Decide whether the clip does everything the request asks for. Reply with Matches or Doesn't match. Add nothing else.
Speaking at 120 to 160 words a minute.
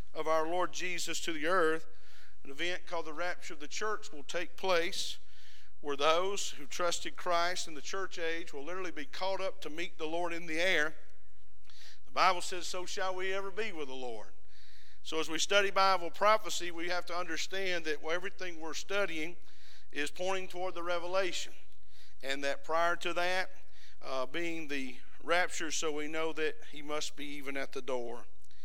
Doesn't match